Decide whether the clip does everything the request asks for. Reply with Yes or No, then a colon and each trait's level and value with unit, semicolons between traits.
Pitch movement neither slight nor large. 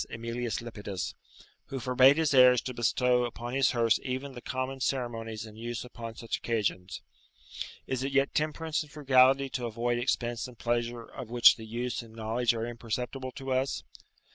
No: narrow, 2.1 semitones